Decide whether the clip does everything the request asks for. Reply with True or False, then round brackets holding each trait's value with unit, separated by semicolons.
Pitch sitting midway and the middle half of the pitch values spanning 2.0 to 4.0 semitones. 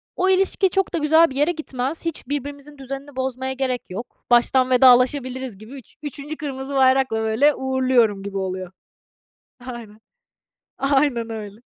False (265 Hz; 3.2 semitones)